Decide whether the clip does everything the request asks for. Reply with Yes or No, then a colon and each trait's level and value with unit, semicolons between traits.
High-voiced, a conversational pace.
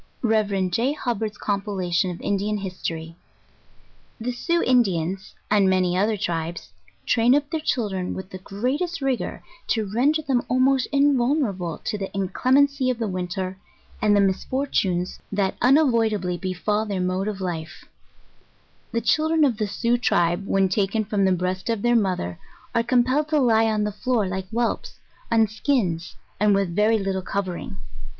Yes: high, 210 Hz; average, 160 wpm